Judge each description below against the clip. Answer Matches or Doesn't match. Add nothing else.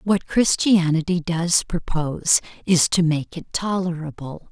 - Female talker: Matches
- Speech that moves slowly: Matches